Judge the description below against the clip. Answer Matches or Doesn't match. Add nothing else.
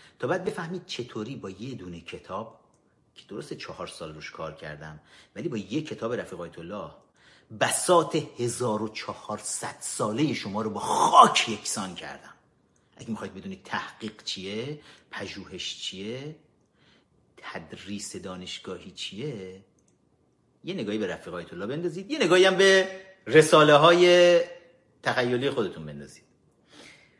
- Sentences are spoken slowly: Doesn't match